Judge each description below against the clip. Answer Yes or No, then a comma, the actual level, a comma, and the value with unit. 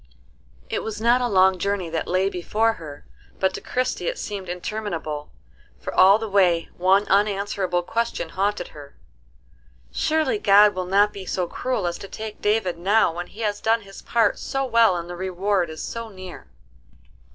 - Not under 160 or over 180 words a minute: Yes, average, 175 wpm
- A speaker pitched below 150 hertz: No, high, 195 Hz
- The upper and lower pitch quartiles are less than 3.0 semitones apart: No, average, 3.5 semitones